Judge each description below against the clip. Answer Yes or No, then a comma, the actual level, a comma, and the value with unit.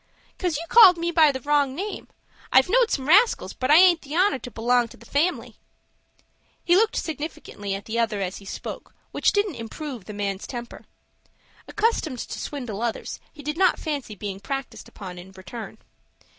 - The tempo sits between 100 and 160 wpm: No, average, 185 wpm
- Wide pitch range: Yes, wide, 7.5 semitones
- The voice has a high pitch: Yes, very high, 275 Hz